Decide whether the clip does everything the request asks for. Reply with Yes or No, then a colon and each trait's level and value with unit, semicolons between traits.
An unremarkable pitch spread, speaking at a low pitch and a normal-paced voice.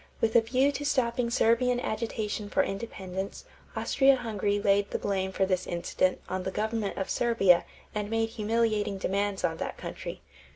No: average, 3.1 semitones; high, 210 Hz; average, 165 wpm